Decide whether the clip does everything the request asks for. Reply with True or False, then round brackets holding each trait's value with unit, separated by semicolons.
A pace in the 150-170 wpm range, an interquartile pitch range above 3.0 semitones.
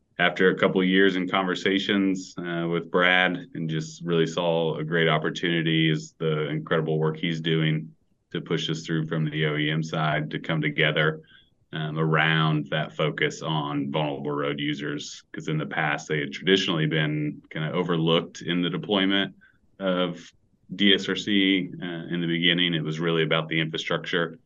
False (165 wpm; 2.5 semitones)